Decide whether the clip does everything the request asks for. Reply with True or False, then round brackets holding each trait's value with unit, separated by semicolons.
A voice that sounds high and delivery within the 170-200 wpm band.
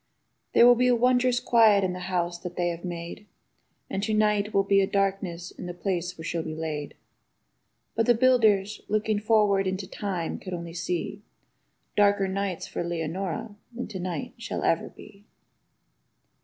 True (195 Hz; 175 wpm)